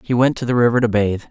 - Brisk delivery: Yes, fast, 325 wpm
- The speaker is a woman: No, male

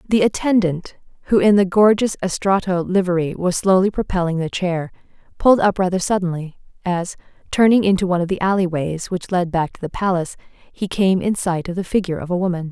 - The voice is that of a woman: Yes, female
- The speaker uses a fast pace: No, average, 195 wpm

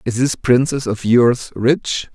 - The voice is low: Yes, low, 120 Hz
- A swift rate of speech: No, average, 170 wpm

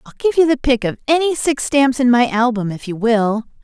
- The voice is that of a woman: Yes, female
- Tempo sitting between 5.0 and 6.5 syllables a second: Yes, 5.4 syllables/s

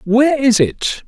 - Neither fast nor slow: Yes, average, 170 wpm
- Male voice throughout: Yes, male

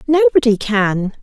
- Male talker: No, female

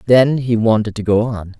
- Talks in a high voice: No, low, 115 Hz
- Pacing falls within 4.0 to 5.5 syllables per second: Yes, 5.0 syllables/s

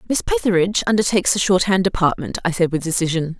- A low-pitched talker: No, medium, 185 Hz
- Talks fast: No, average, 175 wpm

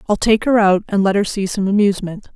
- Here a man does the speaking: No, female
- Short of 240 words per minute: No, fast, 255 wpm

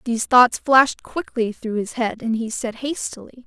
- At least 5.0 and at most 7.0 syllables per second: No, 4.8 syllables/s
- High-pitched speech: Yes, high, 235 Hz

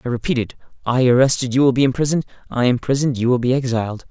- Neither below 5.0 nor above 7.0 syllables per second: No, 7.5 syllables/s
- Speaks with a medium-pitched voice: No, low, 125 Hz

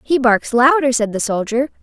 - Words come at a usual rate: Yes, average, 195 wpm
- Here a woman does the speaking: Yes, female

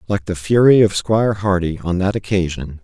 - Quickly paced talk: No, average, 190 wpm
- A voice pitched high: No, very low, 95 Hz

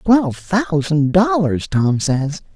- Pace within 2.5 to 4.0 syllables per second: Yes, 3.4 syllables/s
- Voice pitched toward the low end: No, medium, 170 Hz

